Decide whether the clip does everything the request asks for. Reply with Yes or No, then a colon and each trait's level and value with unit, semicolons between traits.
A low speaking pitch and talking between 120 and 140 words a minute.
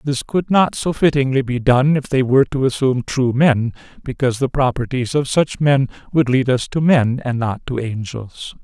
No: low, 130 Hz; average, 200 wpm